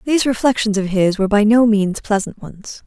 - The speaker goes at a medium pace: No, fast, 210 wpm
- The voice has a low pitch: No, high, 215 Hz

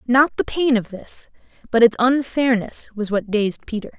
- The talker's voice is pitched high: Yes, high, 235 Hz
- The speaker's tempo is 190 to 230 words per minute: No, average, 180 wpm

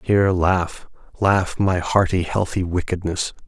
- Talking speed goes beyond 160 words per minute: No, slow, 120 wpm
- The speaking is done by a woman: No, male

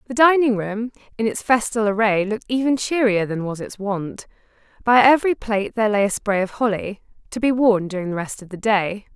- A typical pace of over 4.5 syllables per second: Yes, 5.7 syllables/s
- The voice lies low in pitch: No, high, 215 Hz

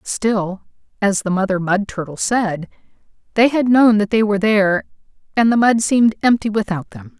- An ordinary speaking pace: Yes, average, 175 wpm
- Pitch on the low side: No, high, 195 Hz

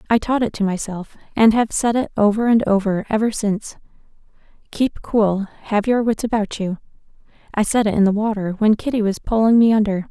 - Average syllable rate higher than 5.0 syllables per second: Yes, 5.5 syllables/s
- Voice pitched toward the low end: No, high, 215 Hz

